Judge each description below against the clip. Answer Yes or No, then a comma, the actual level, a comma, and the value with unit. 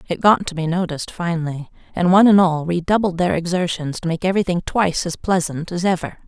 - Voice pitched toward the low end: No, medium, 175 Hz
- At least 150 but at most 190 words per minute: No, average, 200 wpm